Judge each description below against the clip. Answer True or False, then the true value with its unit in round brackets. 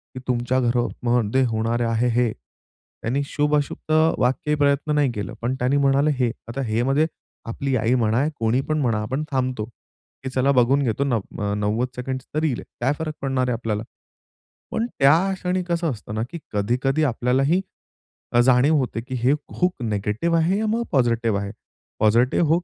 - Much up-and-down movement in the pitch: False (3.7 semitones)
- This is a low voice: True (130 Hz)